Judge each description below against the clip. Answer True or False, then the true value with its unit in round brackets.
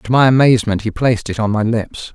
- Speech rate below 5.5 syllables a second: False (6.2 syllables/s)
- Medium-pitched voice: False (115 Hz)